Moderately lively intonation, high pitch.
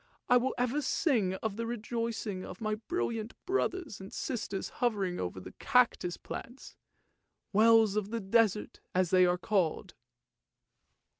Yes: average, 3.9 semitones; high, 220 Hz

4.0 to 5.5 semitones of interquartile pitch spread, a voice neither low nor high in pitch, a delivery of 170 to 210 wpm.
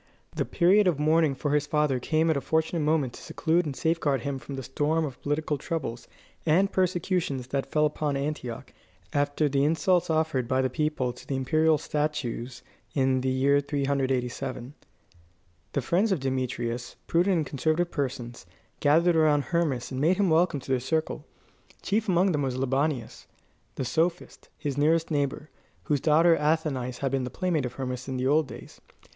No: average, 3.4 semitones; medium, 145 Hz; average, 175 wpm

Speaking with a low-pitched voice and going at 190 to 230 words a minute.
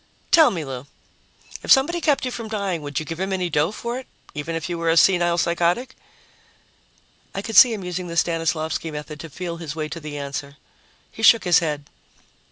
No: medium, 170 Hz; fast, 205 wpm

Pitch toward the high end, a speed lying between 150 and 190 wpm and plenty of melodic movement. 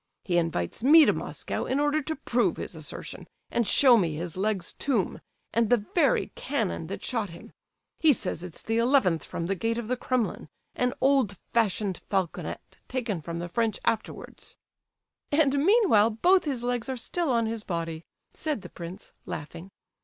Yes: high, 225 Hz; average, 175 wpm; wide, 6.5 semitones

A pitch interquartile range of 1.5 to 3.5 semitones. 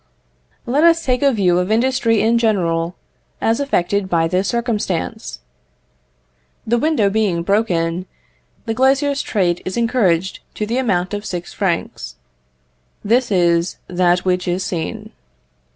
No: average, 5.0 semitones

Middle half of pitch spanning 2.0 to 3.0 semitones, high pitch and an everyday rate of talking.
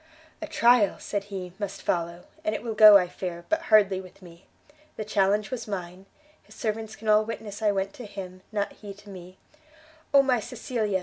Yes: narrow, 2.6 semitones; high, 205 Hz; average, 195 wpm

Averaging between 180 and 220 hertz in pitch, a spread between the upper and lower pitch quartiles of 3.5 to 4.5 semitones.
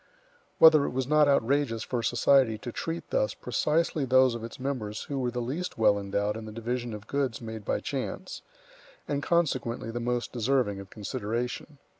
No: low, 125 Hz; average, 3.9 semitones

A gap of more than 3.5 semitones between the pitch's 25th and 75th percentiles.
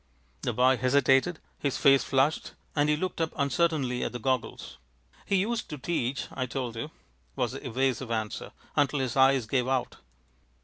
No: average, 2.8 semitones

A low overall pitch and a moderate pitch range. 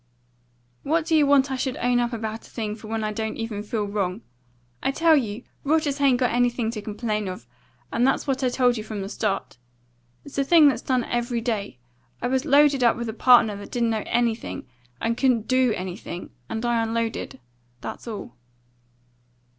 No: high, 235 Hz; average, 3.3 semitones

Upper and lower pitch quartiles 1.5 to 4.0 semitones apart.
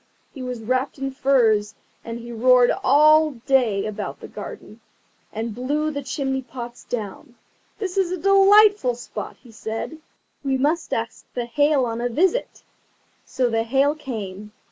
No: average, 4.4 semitones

